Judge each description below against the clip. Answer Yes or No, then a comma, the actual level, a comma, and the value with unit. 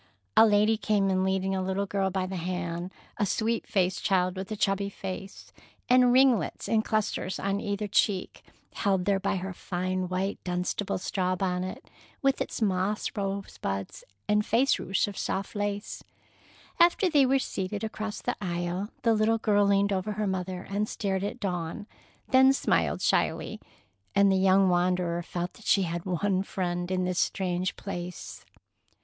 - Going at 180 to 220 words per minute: No, average, 165 wpm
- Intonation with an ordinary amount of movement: No, narrow, 2.2 semitones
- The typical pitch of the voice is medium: No, high, 195 Hz